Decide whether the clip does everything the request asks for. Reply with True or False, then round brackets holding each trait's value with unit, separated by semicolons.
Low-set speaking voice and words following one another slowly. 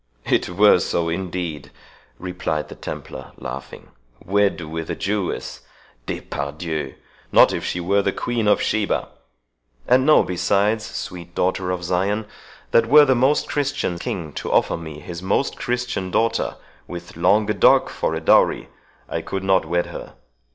False (95 Hz; 145 wpm)